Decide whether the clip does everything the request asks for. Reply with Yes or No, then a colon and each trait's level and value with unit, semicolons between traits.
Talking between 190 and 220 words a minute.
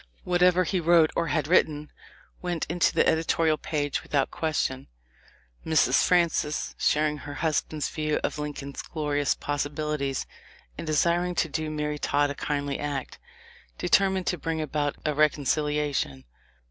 No: average, 140 wpm